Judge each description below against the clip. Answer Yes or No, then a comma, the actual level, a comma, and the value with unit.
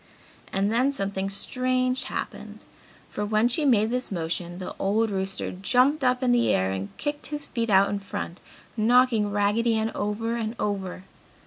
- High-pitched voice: Yes, high, 220 Hz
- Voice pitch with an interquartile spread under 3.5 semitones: No, average, 4.2 semitones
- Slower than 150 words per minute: No, average, 165 wpm